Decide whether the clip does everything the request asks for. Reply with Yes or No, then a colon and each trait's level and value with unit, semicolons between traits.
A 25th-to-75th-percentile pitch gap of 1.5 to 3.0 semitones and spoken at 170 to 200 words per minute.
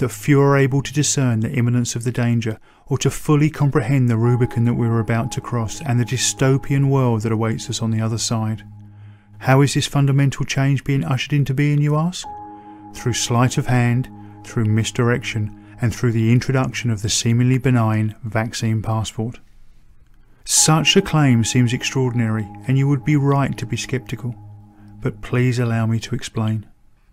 No: average, 3.6 semitones; average, 175 wpm